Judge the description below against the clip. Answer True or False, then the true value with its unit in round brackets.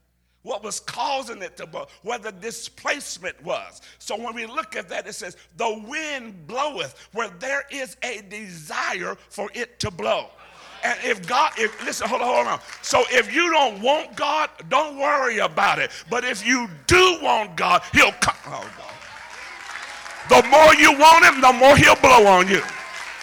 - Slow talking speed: False (180 wpm)